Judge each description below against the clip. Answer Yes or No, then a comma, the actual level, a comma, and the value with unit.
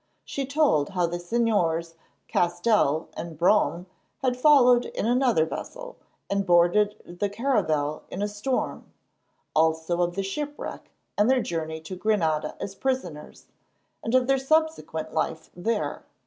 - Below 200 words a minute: Yes, slow, 135 wpm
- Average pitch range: No, wide, 7.0 semitones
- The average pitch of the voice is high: Yes, high, 195 Hz